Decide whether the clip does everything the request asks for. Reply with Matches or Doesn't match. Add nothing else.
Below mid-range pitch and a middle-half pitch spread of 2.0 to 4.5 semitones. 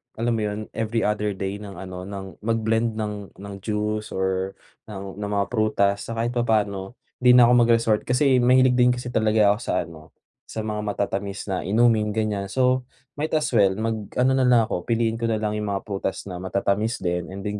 Matches